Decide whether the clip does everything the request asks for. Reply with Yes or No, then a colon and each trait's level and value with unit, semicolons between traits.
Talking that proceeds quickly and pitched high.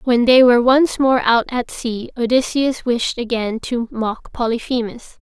No: average, 160 wpm; high, 245 Hz